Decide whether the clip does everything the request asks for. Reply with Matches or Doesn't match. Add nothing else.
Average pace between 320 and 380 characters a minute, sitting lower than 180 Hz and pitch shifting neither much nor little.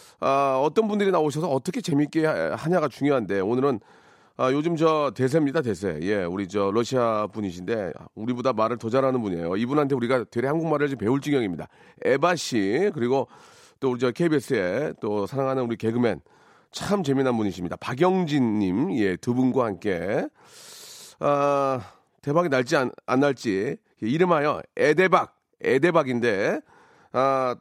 Matches